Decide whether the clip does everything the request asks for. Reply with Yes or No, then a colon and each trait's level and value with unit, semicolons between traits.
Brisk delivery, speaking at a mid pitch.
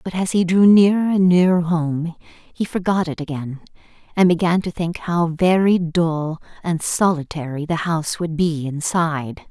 No: average, 165 wpm; medium, 170 Hz